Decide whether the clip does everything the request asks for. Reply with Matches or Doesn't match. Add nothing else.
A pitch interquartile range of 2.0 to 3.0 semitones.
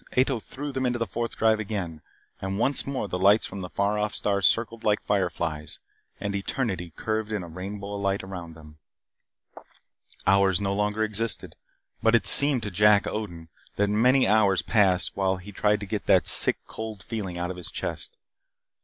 Matches